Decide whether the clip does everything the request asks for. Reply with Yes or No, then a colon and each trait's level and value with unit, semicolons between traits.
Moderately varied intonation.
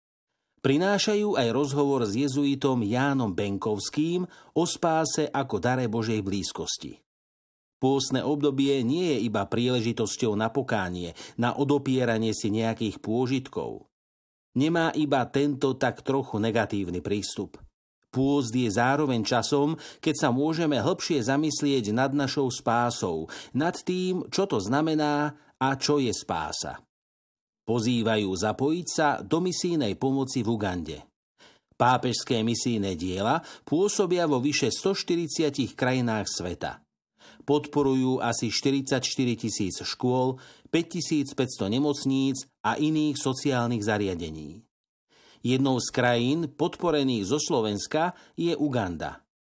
Yes: average, 4.3 semitones